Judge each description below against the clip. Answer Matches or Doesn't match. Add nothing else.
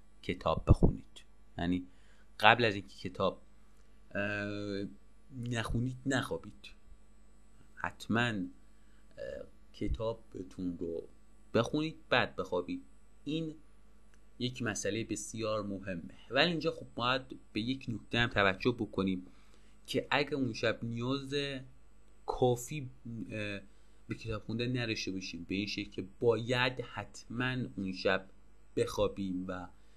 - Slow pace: Matches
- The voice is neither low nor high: Doesn't match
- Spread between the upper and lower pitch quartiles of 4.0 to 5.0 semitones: Matches